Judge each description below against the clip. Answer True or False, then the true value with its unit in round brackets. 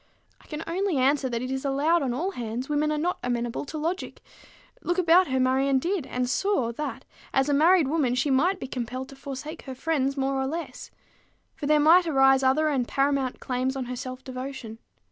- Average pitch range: True (3.2 semitones)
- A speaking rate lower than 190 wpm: False (205 wpm)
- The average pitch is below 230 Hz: False (275 Hz)